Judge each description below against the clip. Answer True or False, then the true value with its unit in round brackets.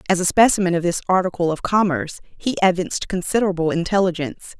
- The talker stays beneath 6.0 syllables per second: False (6.9 syllables/s)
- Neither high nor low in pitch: True (180 Hz)